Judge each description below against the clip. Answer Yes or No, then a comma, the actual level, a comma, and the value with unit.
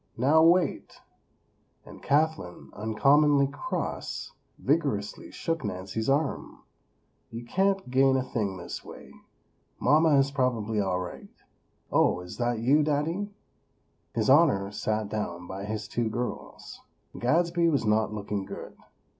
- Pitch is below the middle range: Yes, low, 125 Hz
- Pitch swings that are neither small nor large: No, wide, 6.0 semitones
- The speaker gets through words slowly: Yes, slow, 125 wpm